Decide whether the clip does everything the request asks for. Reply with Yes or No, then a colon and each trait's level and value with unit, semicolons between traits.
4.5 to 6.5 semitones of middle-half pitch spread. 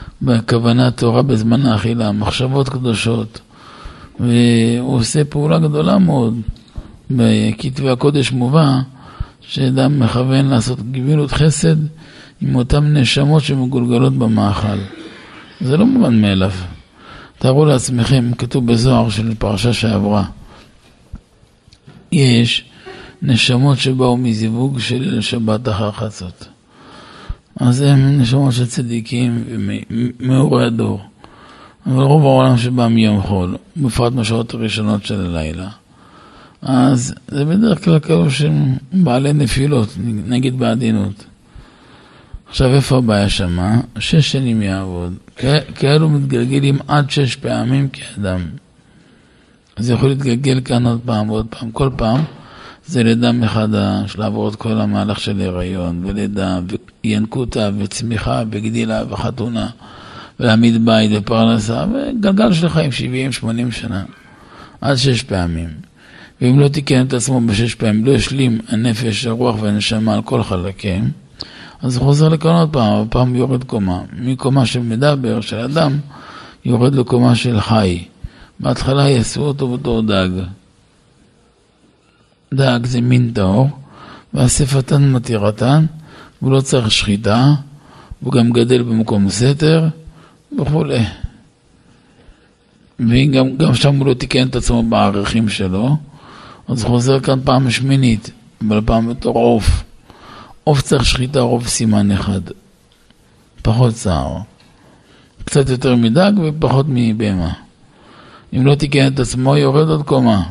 No: average, 3.8 semitones